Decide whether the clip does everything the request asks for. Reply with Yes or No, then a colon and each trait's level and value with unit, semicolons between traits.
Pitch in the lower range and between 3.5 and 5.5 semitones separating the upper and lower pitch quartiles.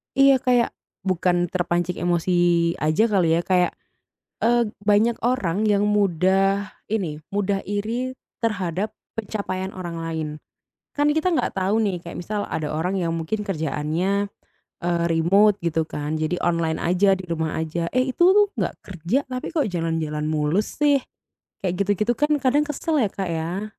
No: high, 190 Hz; average, 4.4 semitones